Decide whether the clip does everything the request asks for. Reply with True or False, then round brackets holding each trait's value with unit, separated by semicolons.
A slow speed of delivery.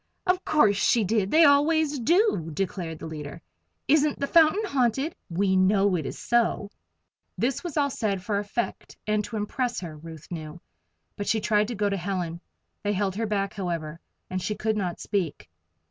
False (180 wpm)